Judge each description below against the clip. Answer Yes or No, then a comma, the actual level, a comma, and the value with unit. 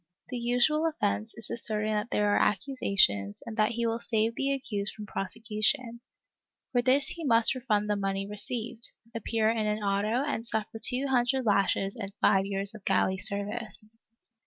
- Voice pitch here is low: No, high, 220 Hz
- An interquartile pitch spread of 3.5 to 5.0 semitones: No, average, 3.0 semitones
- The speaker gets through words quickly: No, average, 175 wpm